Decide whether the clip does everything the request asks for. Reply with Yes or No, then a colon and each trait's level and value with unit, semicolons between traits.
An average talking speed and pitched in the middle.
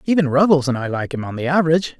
No: fast, 270 wpm; medium, 150 Hz